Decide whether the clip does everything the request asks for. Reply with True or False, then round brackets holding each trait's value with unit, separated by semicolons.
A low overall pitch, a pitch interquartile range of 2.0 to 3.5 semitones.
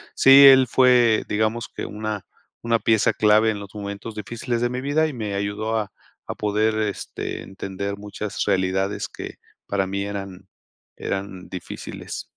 True (105 Hz; 2.6 semitones)